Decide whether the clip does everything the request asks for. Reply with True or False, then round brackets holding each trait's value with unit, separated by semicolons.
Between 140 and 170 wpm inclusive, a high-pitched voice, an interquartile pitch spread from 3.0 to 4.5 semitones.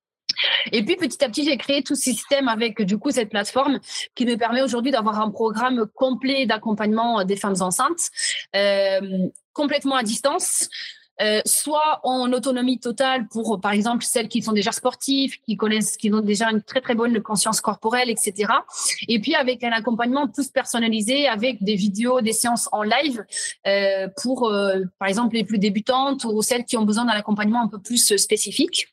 False (185 wpm; 235 Hz; 3.6 semitones)